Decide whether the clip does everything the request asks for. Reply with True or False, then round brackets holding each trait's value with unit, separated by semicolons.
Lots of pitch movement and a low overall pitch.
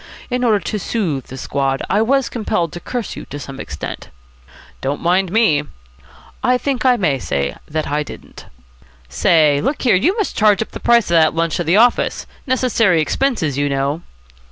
False (8.4 semitones; 175 Hz)